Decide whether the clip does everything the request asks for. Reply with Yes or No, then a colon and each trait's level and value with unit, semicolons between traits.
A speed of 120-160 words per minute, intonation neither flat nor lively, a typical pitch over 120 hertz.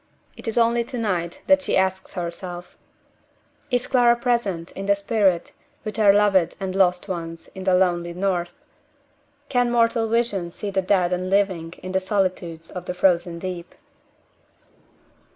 Yes: average, 155 wpm; average, 3.4 semitones; high, 190 Hz